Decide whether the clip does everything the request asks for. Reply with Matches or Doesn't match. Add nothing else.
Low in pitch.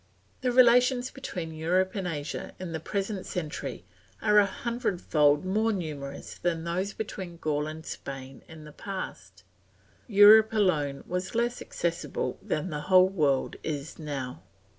Doesn't match